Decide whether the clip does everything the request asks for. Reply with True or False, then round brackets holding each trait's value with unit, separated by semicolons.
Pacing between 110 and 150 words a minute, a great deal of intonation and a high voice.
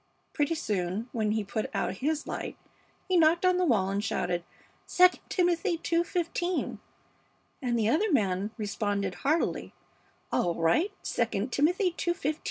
True (140 wpm; 9.0 semitones; 270 Hz)